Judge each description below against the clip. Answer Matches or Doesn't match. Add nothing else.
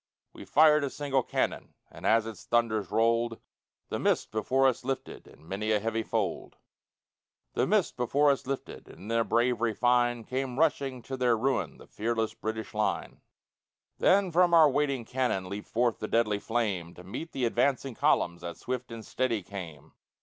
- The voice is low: Matches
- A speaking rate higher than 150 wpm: Matches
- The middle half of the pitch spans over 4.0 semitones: Doesn't match